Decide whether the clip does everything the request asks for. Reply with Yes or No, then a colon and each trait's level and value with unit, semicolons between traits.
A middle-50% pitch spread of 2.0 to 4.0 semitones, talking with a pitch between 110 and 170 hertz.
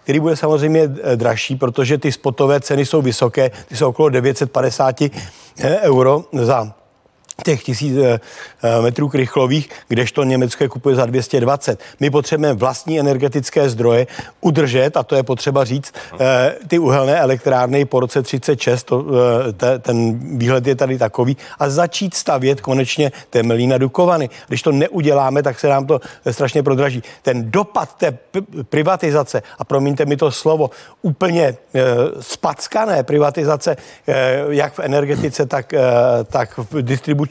Yes: narrow, 2.5 semitones; medium, 140 Hz